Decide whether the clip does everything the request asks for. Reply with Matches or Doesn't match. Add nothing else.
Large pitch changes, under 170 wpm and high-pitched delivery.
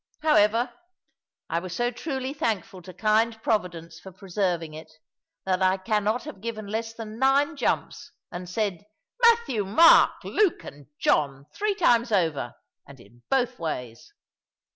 Matches